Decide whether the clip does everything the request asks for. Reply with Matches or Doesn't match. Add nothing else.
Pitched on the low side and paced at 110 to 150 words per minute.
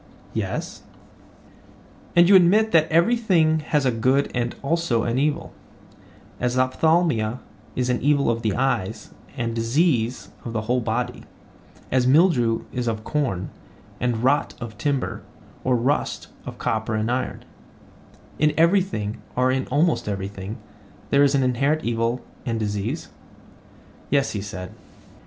Matches